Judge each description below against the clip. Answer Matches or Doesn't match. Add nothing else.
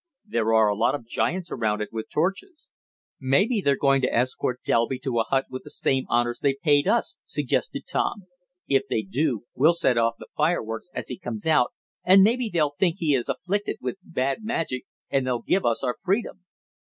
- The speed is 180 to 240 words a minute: Matches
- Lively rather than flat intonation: Matches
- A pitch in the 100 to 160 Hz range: Matches